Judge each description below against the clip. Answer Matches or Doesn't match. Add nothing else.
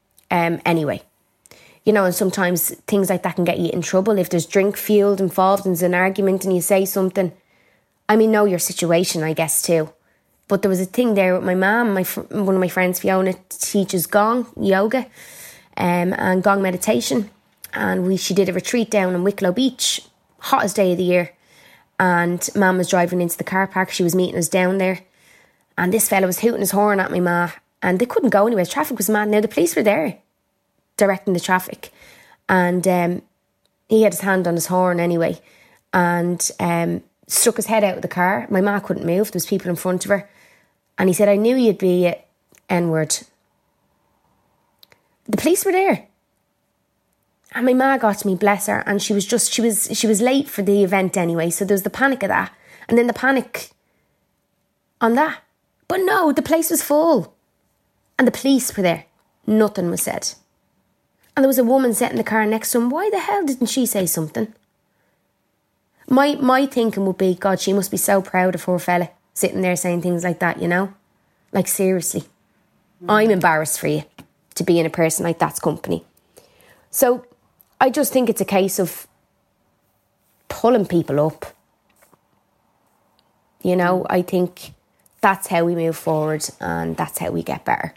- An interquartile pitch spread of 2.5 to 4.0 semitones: Matches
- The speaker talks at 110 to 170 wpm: Doesn't match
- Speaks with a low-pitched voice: Doesn't match